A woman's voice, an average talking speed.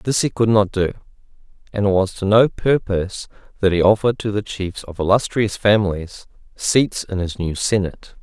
No: male; average, 180 wpm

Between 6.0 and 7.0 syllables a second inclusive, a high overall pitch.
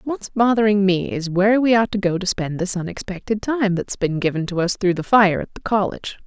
No: 5.6 syllables/s; high, 195 Hz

